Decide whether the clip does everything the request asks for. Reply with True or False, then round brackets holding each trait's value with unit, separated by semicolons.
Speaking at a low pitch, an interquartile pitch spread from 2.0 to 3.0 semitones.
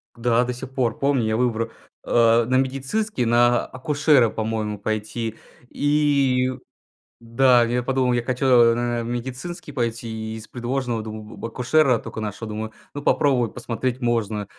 True (120 Hz; 2.4 semitones)